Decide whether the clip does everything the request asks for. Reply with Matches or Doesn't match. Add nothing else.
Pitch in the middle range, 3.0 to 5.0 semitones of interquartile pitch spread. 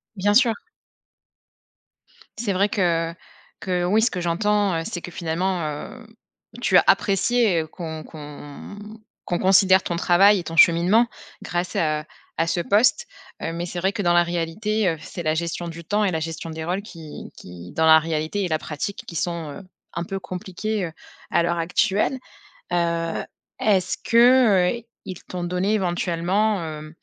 Matches